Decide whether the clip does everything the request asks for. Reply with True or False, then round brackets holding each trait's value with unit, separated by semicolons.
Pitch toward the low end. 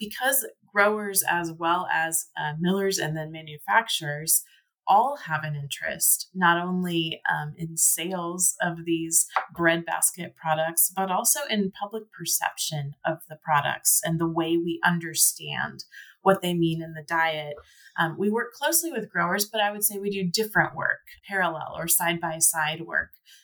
False (170 Hz)